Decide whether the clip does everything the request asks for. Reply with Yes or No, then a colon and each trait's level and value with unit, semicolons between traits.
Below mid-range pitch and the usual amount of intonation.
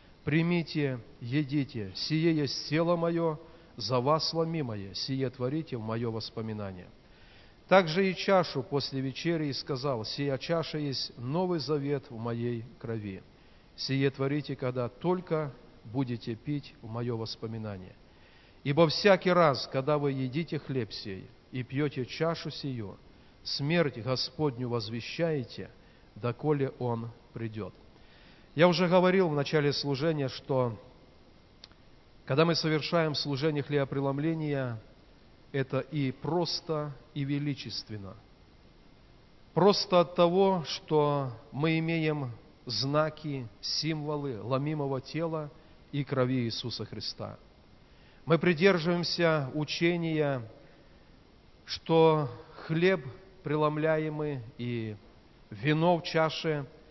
No: medium, 145 Hz; average, 4.8 semitones